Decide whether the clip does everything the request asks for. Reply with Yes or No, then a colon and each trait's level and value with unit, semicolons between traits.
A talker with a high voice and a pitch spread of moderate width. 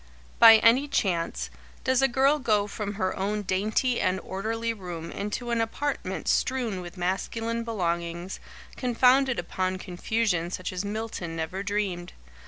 Yes: high, 205 Hz; average, 4.0 semitones